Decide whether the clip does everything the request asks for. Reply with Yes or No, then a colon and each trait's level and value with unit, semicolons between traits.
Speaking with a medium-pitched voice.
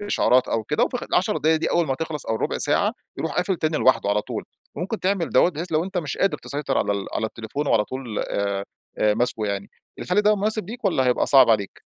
Yes: medium, 150 Hz